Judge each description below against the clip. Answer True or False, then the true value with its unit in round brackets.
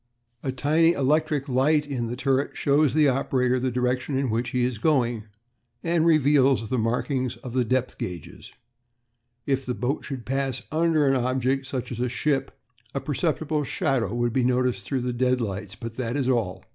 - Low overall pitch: True (130 Hz)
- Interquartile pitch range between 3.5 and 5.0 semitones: False (2.5 semitones)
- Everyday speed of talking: True (180 wpm)